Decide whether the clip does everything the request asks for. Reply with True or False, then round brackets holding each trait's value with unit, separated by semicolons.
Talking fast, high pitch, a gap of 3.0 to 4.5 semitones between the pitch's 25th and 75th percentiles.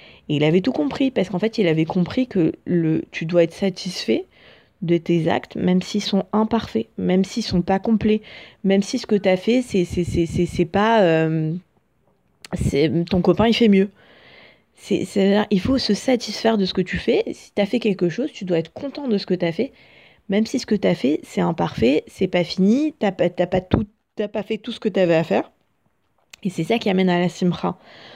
True (235 wpm; 195 Hz; 3.7 semitones)